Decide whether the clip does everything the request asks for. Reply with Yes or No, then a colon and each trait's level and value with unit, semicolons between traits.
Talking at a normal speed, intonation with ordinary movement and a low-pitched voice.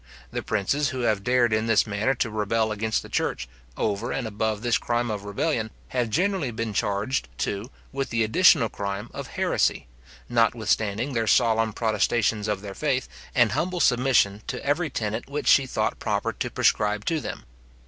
Yes: average, 175 wpm; average, 3.2 semitones; low, 115 Hz